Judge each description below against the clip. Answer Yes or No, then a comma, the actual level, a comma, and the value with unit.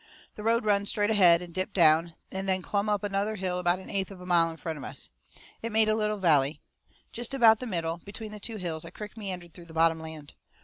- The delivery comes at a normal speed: No, fast, 250 wpm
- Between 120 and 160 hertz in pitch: No, high, 190 Hz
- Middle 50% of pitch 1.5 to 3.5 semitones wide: No, average, 4.0 semitones